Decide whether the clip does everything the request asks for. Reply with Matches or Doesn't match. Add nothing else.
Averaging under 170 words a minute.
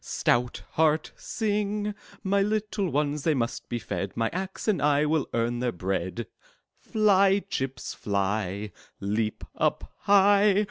Matches